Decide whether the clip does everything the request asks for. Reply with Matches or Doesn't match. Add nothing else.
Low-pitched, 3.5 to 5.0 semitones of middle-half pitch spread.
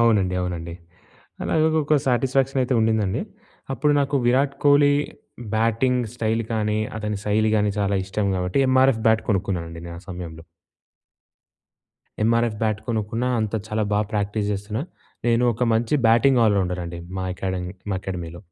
Matches